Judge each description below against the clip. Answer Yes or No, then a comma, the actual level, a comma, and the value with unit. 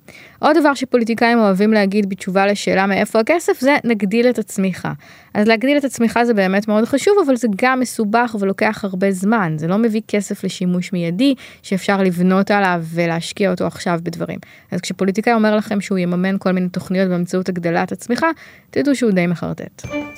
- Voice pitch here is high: Yes, high, 205 Hz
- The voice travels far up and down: No, average, 3.9 semitones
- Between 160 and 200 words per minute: Yes, fast, 170 wpm